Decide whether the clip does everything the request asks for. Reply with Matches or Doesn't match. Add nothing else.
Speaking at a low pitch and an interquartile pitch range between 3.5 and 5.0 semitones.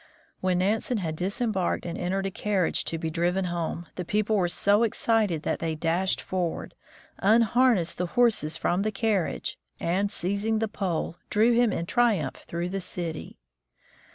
Doesn't match